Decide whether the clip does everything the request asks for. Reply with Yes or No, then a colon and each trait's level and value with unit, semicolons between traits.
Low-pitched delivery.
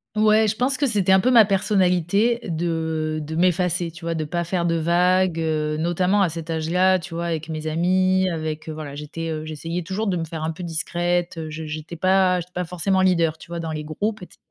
No: medium, 170 Hz